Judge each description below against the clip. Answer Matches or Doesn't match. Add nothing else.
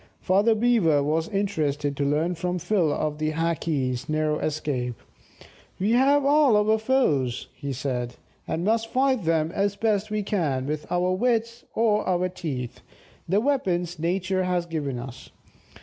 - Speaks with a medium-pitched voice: Matches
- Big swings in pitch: Matches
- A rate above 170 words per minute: Doesn't match